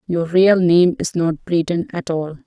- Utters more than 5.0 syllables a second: No, 4.1 syllables/s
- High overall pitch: No, medium, 170 Hz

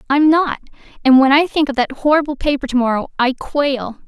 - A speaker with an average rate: Yes, average, 175 wpm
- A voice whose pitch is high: Yes, very high, 275 Hz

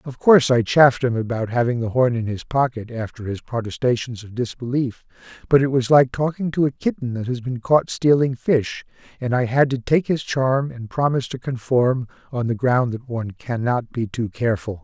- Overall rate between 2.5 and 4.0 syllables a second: No, 5.3 syllables/s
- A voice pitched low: Yes, low, 125 Hz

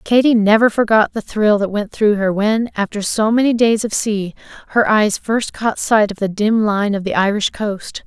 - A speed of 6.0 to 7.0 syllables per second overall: No, 4.6 syllables/s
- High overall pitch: Yes, high, 210 Hz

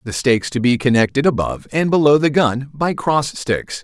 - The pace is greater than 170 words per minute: Yes, fast, 205 wpm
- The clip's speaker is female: No, male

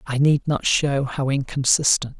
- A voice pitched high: No, low, 135 Hz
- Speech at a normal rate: Yes, average, 165 wpm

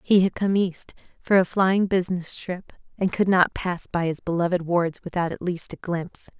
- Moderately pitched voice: Yes, medium, 180 Hz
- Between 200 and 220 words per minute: Yes, fast, 205 wpm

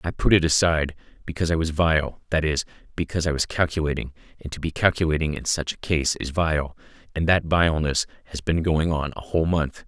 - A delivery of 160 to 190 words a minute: No, fast, 205 wpm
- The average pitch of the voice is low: Yes, very low, 80 Hz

